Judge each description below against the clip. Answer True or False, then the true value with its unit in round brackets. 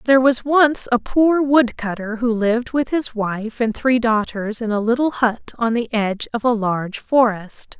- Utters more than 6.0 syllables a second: False (4.5 syllables/s)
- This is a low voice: False (235 Hz)